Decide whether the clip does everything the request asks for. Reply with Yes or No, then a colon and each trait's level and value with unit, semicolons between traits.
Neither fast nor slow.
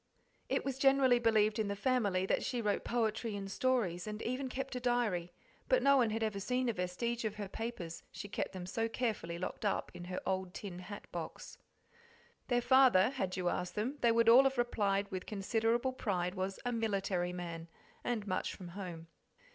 Yes: average, 195 wpm